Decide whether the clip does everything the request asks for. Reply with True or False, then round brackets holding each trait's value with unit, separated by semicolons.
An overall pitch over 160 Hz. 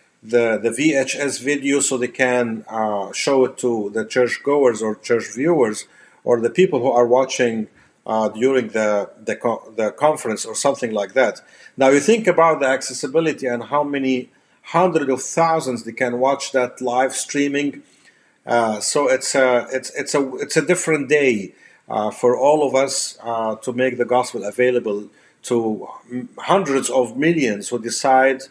False (130 Hz)